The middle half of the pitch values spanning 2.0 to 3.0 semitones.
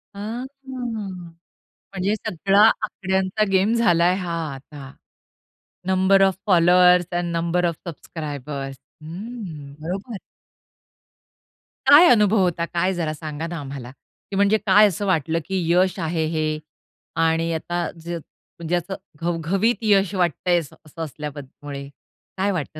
No: average, 3.4 semitones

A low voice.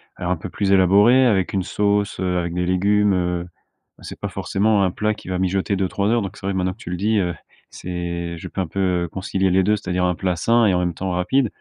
Yes: very low, 95 Hz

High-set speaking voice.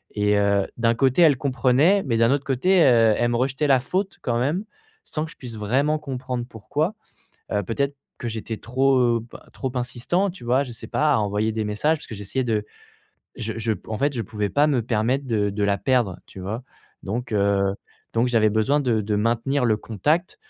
No: low, 120 Hz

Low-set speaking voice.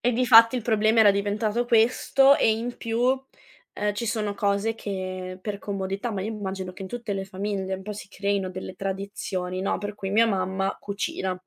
No: high, 200 Hz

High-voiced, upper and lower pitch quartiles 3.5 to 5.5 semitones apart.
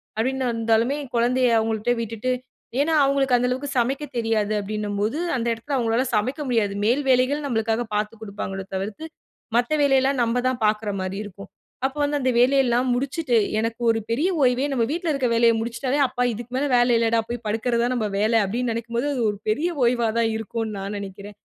No: high, 235 Hz; average, 2.8 semitones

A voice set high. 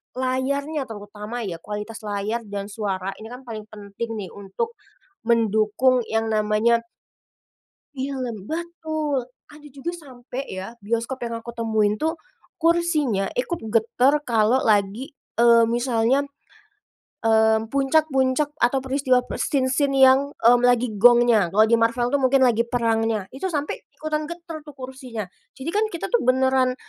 Yes: high, 245 Hz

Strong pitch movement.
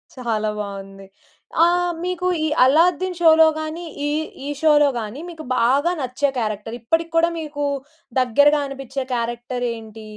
Yes: wide, 5.7 semitones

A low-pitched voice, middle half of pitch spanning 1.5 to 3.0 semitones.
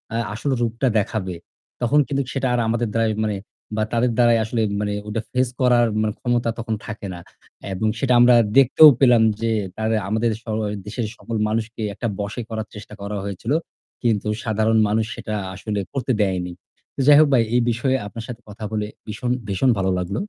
Yes: low, 110 Hz; narrow, 2.5 semitones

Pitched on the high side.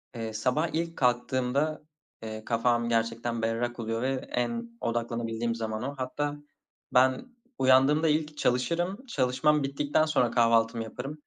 No: low, 125 Hz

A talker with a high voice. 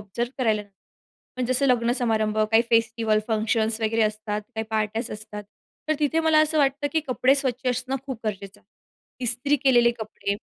Yes: high, 230 Hz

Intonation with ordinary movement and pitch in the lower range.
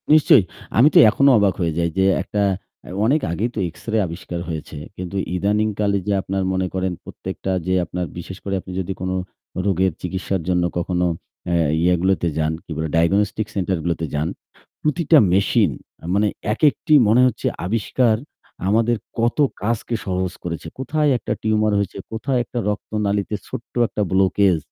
Yes: average, 3.3 semitones; low, 100 Hz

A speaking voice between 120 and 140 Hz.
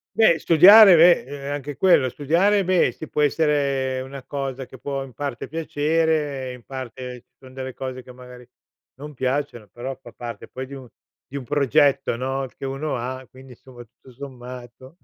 Yes: low, 135 Hz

